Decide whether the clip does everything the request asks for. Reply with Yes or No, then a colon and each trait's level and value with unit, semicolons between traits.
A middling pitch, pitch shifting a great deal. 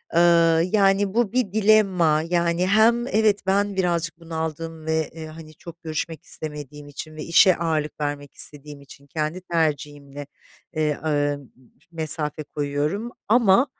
No: medium, 165 Hz; average, 4.1 semitones